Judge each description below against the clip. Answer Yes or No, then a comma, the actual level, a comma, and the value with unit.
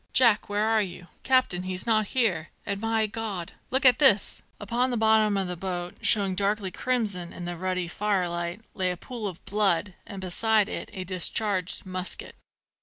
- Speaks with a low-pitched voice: No, high, 200 Hz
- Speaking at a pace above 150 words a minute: Yes, average, 180 wpm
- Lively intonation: No, average, 3.3 semitones